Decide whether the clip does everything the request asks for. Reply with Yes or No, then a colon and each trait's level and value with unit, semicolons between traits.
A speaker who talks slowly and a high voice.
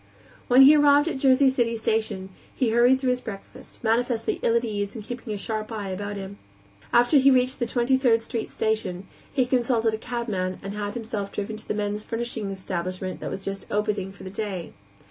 No: fast, 205 wpm; high, 220 Hz